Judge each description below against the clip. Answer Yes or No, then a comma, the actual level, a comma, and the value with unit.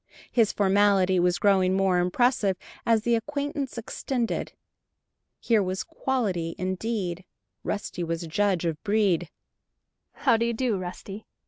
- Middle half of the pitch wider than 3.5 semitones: Yes, average, 4.1 semitones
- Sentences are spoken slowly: Yes, slow, 130 wpm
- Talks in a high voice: Yes, high, 200 Hz